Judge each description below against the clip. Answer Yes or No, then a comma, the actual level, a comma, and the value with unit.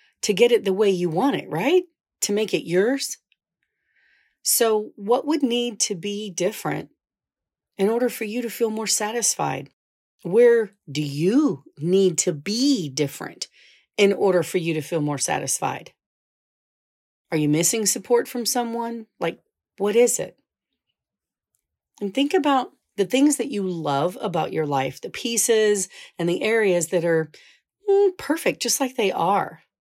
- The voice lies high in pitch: Yes, high, 210 Hz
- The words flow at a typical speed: Yes, average, 155 wpm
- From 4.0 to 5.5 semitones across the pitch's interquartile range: Yes, average, 5.2 semitones